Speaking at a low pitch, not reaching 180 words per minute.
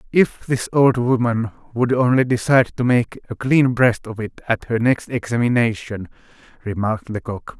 Yes: low, 120 Hz; average, 160 wpm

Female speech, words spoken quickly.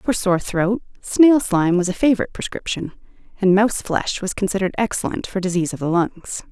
No: female; average, 185 wpm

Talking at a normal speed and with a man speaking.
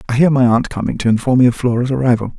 No: fast, 275 wpm; male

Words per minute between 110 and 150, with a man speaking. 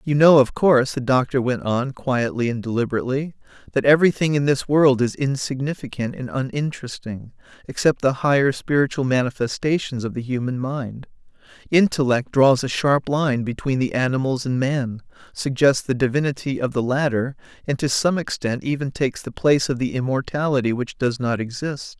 No: average, 165 wpm; male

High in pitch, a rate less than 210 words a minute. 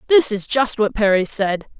Yes: high, 220 Hz; average, 200 wpm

